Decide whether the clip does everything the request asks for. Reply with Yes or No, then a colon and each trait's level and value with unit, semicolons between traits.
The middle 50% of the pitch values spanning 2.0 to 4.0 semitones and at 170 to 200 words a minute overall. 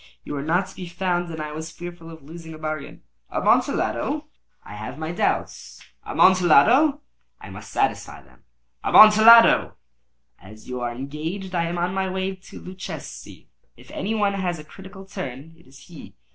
Yes: average, 3.7 semitones; average, 175 wpm